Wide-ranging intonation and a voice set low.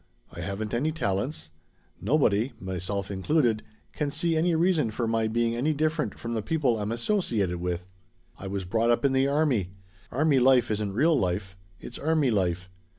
Yes: wide, 7.1 semitones; low, 115 Hz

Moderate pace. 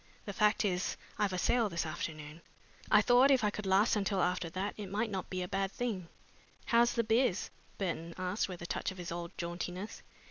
No: fast, 210 wpm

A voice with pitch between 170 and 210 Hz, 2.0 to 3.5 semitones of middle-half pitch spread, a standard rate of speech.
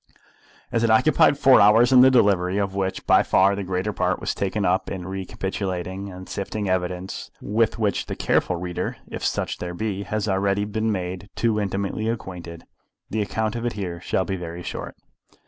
No: low, 100 Hz; average, 2.7 semitones; average, 185 wpm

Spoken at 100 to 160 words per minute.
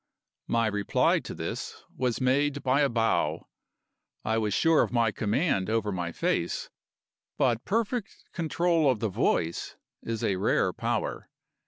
Yes: average, 145 wpm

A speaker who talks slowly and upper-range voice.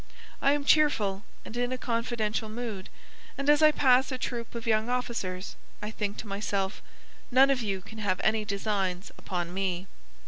No: average, 175 wpm; high, 220 Hz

